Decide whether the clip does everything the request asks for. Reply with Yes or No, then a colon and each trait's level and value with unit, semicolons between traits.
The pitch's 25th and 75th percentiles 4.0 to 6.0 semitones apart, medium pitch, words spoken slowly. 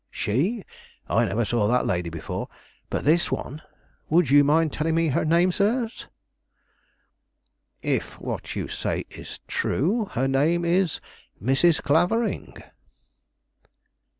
Yes: average, 4.8 semitones; medium, 160 Hz; slow, 125 wpm